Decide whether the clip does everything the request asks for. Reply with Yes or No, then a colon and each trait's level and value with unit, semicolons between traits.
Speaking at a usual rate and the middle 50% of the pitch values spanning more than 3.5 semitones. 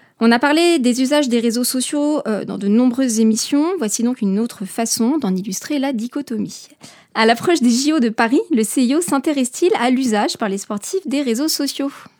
Yes: average, 185 wpm; average, 4.3 semitones